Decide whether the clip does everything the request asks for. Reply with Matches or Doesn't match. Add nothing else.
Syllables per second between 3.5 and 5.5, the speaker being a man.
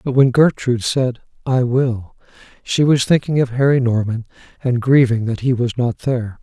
Matches